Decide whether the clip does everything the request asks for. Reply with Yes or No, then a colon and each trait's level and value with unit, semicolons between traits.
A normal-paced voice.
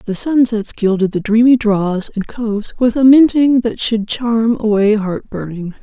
Yes: average, 175 wpm